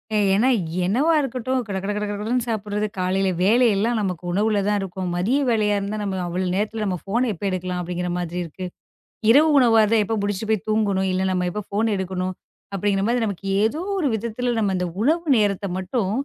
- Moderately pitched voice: No, high, 205 Hz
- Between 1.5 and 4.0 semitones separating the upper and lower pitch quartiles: Yes, average, 3.2 semitones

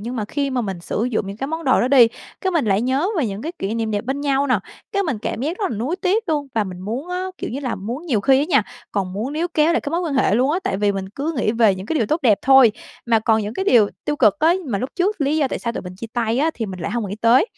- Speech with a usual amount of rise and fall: No, wide, 5.8 semitones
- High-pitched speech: Yes, very high, 250 Hz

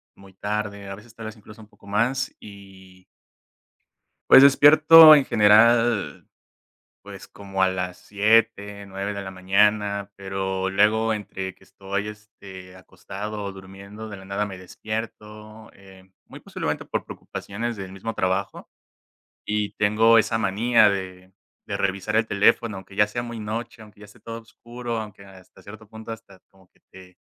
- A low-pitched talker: Yes, low, 105 Hz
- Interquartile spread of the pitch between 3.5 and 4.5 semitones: No, narrow, 2.4 semitones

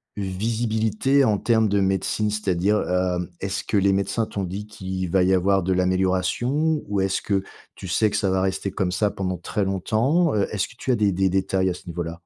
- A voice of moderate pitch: No, very low, 95 Hz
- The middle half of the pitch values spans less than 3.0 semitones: Yes, narrow, 2.4 semitones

